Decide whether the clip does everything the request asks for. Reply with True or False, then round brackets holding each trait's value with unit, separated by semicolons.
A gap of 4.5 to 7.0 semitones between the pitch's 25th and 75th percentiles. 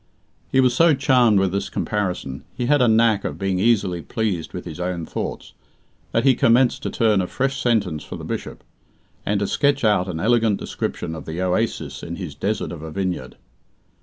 True (4.9 semitones)